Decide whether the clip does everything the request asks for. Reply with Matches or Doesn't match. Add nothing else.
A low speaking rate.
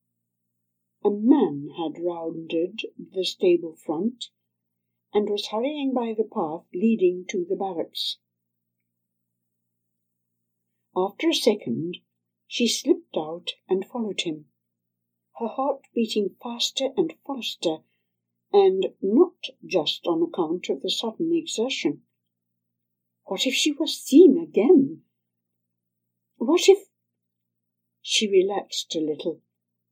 Matches